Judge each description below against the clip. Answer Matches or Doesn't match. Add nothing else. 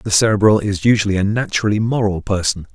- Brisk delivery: Doesn't match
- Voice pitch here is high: Doesn't match